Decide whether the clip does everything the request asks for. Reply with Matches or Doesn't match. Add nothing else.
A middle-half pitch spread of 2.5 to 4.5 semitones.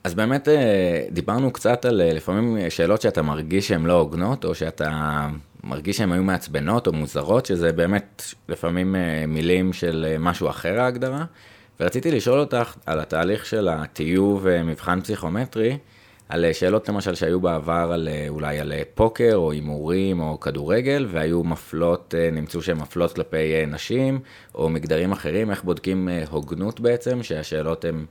Doesn't match